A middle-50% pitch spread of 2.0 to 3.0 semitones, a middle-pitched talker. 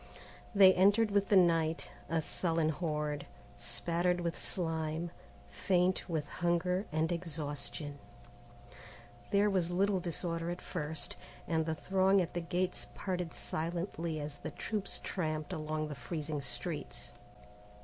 Yes: average, 2.7 semitones; medium, 170 Hz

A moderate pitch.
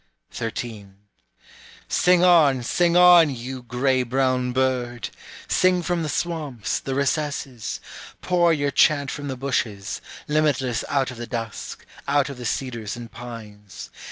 No: low, 130 Hz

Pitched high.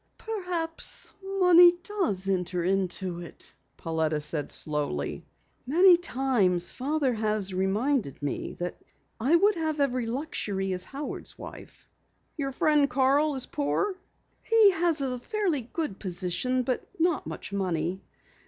Yes: very high, 255 Hz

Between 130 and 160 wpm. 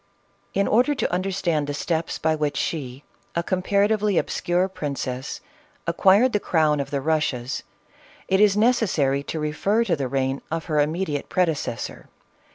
Yes: average, 150 wpm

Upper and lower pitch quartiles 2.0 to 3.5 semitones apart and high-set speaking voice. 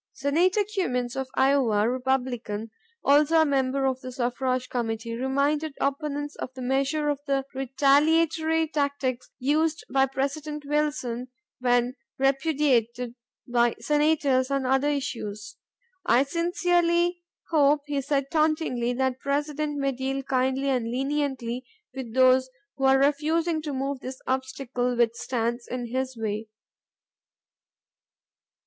Yes: average, 2.8 semitones; very high, 270 Hz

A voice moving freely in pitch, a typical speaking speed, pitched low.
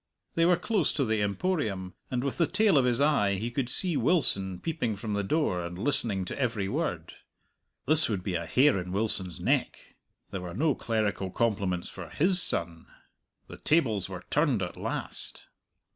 Yes: wide, 7.7 semitones; average, 180 wpm; low, 110 Hz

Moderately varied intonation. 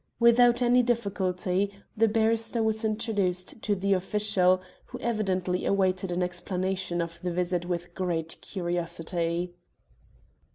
Yes: average, 3.5 semitones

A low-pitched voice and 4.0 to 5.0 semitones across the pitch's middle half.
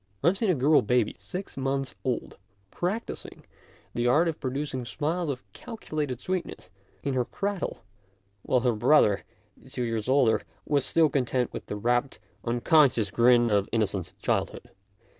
Yes: low, 130 Hz; average, 4.4 semitones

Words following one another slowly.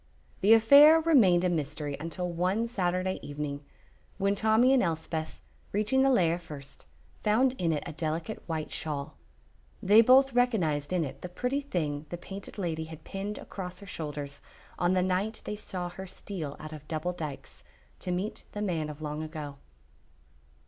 No: average, 170 wpm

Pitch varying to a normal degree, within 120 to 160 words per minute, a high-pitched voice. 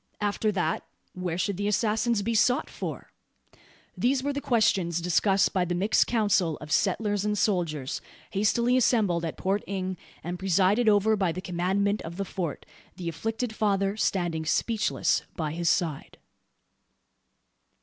Yes: average, 3.6 semitones; average, 150 wpm; high, 195 Hz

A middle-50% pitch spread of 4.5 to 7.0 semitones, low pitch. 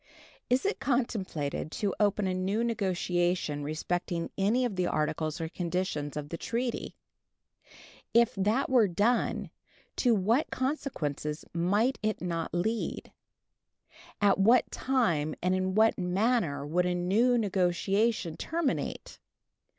No: average, 5.2 semitones; high, 190 Hz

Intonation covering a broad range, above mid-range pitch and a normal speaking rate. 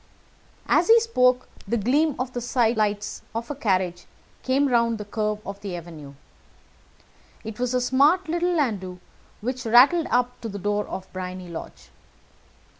No: average, 4.5 semitones; high, 235 Hz; average, 155 wpm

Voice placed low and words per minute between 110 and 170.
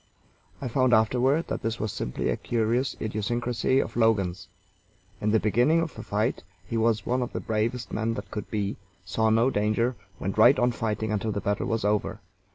No: low, 115 Hz; average, 190 wpm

